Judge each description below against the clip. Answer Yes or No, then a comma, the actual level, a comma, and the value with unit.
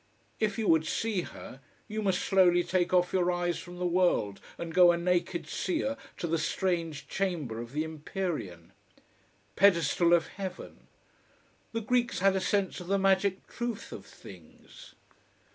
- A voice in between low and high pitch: Yes, medium, 180 Hz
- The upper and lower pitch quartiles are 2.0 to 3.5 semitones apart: Yes, average, 2.9 semitones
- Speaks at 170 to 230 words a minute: No, average, 160 wpm